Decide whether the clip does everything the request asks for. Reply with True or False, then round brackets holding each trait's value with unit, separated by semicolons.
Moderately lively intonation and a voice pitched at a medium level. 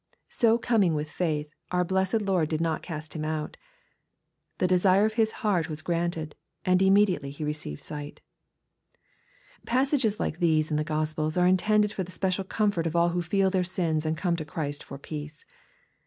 True (3.7 semitones; 170 Hz)